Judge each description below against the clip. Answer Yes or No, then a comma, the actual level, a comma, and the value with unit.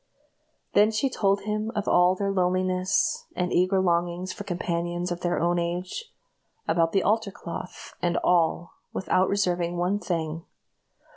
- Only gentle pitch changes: Yes, narrow, 2.2 semitones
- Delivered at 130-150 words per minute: Yes, average, 145 wpm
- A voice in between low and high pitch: Yes, medium, 180 Hz